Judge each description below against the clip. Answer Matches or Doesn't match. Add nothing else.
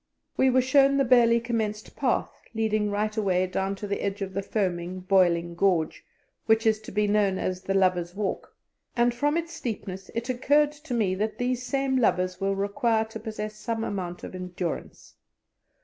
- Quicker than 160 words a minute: Matches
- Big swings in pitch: Doesn't match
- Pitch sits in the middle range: Doesn't match